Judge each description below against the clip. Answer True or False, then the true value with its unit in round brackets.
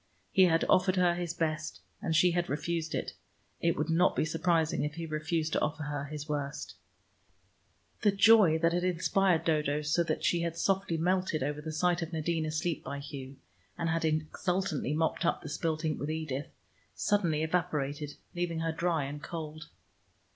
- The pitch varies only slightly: True (2.3 semitones)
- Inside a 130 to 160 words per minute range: False (180 wpm)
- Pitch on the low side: False (160 Hz)